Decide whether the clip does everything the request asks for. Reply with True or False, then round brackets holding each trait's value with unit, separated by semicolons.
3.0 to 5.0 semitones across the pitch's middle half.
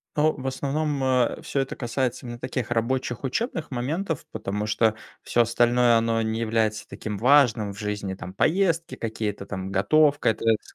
True (4.2 semitones)